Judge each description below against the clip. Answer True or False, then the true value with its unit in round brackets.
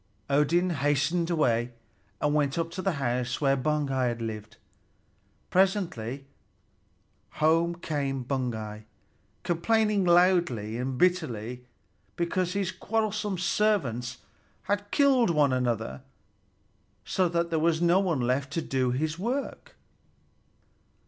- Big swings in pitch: True (6.1 semitones)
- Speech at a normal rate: False (110 wpm)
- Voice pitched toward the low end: False (155 Hz)